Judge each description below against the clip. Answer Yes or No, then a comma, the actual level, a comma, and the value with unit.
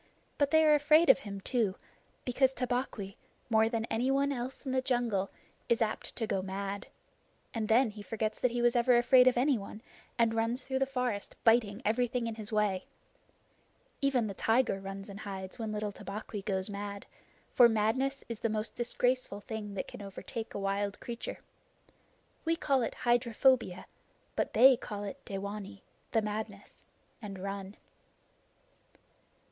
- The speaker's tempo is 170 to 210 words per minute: No, average, 160 wpm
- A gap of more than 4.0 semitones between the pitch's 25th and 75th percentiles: No, average, 3.6 semitones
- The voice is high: Yes, high, 225 Hz